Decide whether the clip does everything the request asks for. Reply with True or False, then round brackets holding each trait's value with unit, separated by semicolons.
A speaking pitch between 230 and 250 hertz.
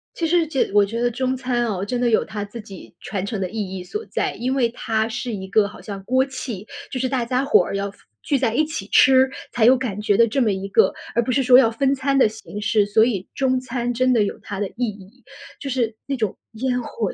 True (235 Hz)